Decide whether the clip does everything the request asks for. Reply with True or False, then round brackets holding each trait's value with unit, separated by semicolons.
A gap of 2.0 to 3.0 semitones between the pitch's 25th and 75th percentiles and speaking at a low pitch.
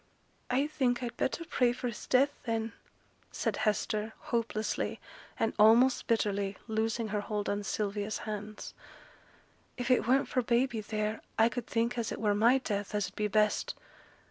False (2.5 semitones; 225 Hz)